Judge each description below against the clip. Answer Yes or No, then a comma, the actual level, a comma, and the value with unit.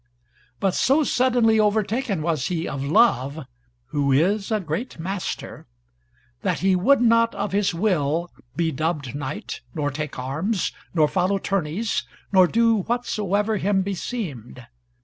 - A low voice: No, high, 190 Hz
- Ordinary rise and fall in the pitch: No, wide, 6.1 semitones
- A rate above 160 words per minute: No, slow, 135 wpm